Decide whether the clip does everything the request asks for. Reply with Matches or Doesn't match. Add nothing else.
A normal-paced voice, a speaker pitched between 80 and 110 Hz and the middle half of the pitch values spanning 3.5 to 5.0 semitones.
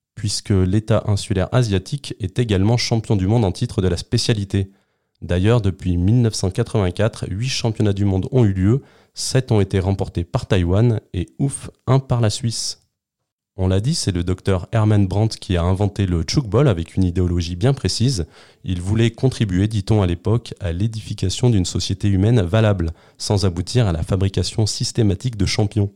Matches